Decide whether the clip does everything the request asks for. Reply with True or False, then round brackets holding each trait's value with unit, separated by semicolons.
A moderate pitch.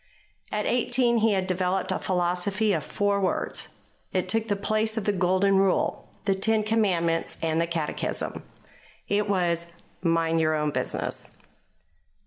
False (195 Hz)